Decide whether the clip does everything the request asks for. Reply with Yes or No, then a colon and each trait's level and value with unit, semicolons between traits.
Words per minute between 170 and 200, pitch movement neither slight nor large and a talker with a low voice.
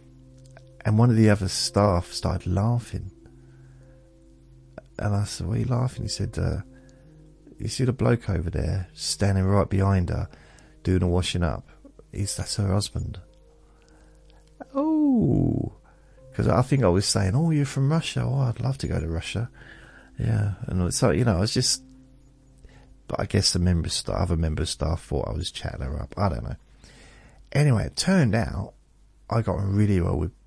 No: average, 175 wpm; wide, 7.0 semitones; low, 100 Hz